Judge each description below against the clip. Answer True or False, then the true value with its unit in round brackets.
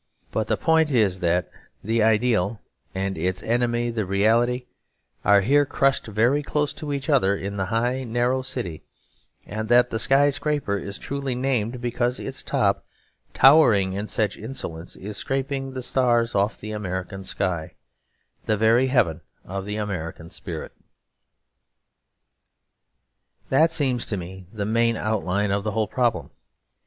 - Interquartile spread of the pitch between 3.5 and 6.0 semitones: True (4.5 semitones)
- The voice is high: False (110 Hz)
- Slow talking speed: False (145 wpm)